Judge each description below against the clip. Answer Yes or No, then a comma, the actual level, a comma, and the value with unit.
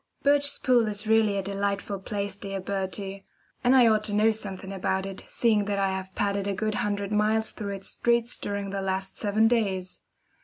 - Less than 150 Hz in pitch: No, high, 200 Hz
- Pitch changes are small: Yes, narrow, 1.9 semitones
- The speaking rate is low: No, average, 190 wpm